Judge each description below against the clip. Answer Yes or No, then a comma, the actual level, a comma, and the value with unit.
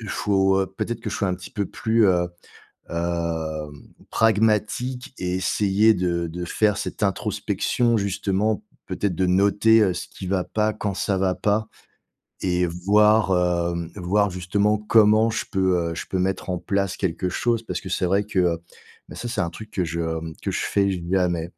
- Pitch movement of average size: Yes, average, 3.0 semitones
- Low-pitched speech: Yes, very low, 95 Hz